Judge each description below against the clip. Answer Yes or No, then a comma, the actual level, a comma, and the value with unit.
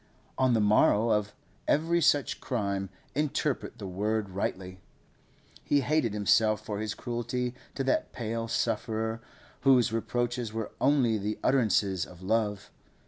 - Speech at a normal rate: No, slow, 125 wpm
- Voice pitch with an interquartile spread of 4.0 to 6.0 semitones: No, average, 3.1 semitones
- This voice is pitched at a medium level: No, low, 110 Hz